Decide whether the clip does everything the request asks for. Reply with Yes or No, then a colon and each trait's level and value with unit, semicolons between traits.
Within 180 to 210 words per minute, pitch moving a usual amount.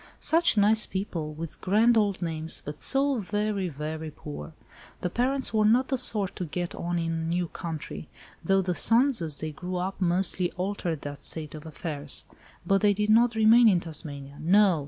Yes: average, 185 wpm; average, 4.9 semitones